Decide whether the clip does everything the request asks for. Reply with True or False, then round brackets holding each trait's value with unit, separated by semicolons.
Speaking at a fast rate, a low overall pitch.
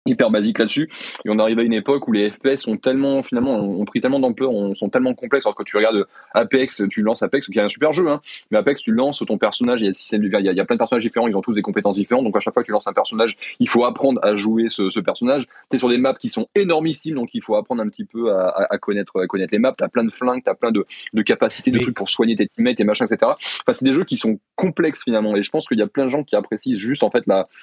True (310 wpm; 130 Hz)